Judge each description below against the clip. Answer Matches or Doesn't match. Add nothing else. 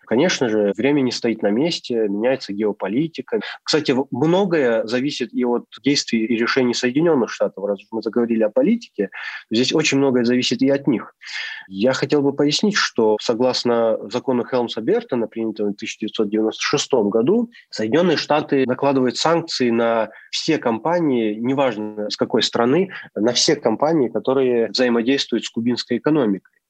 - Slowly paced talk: Doesn't match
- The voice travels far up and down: Doesn't match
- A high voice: Doesn't match